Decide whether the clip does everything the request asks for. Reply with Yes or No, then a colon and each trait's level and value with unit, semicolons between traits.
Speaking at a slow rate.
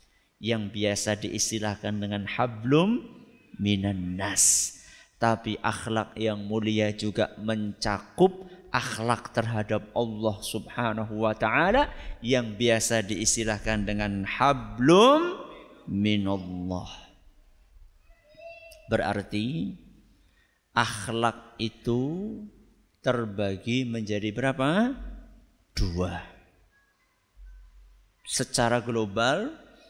Yes: slow, 65 wpm